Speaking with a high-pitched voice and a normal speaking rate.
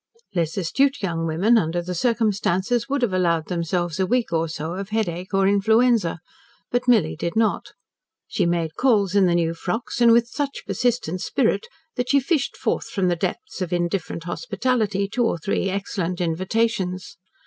Yes: high, 195 Hz; average, 170 wpm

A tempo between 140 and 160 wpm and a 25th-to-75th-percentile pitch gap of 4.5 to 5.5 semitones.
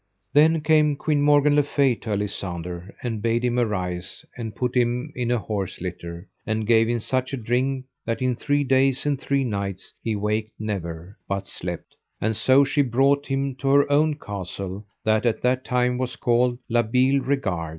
No: average, 185 wpm; average, 4.8 semitones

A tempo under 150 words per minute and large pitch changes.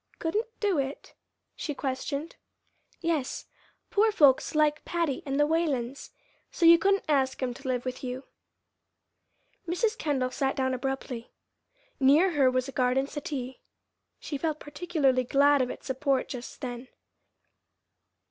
No: average, 140 wpm; average, 3.6 semitones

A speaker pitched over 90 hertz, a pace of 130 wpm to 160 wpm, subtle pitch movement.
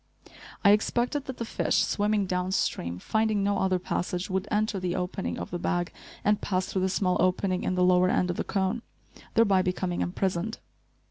No: high, 190 Hz; average, 185 wpm; narrow, 2.3 semitones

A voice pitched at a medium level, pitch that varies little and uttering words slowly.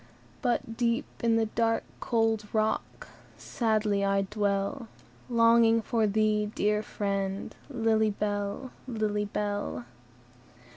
No: high, 215 Hz; narrow, 1.9 semitones; slow, 105 wpm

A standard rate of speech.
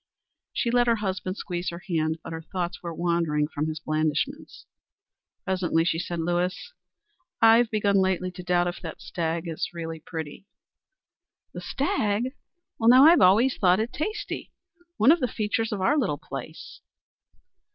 Yes: average, 160 wpm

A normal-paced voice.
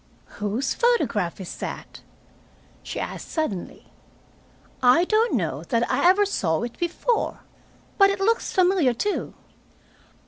No: slow, 125 wpm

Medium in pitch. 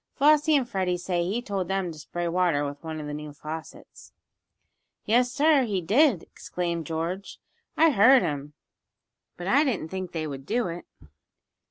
Yes: medium, 180 Hz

